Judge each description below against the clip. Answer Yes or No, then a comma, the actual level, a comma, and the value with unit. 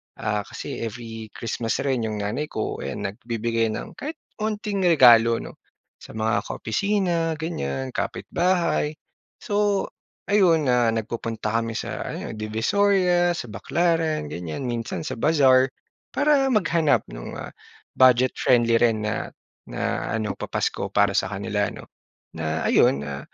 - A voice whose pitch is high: No, low, 120 Hz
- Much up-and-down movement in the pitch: Yes, wide, 7.5 semitones